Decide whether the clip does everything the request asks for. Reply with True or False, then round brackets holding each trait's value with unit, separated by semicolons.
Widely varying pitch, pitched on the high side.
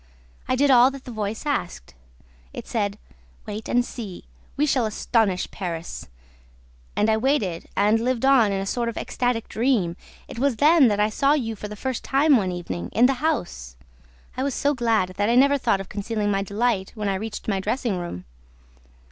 False (4.4 semitones; 225 Hz)